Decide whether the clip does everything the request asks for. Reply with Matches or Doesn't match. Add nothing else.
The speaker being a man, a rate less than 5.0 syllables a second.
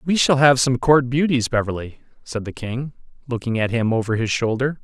Doesn't match